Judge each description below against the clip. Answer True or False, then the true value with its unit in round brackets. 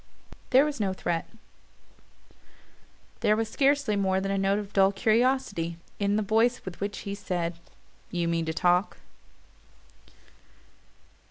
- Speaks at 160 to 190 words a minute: False (140 wpm)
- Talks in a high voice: True (200 Hz)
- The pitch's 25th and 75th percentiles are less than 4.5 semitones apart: True (3.4 semitones)